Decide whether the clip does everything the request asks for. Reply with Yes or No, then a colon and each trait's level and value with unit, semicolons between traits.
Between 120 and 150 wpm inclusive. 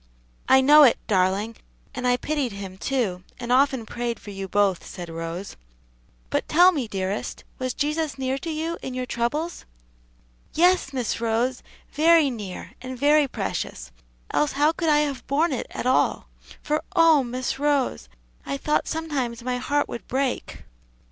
No: average, 160 wpm